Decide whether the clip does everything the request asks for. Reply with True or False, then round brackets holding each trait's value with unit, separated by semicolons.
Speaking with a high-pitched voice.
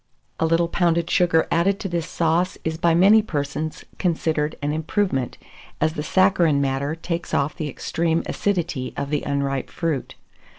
False (160 Hz)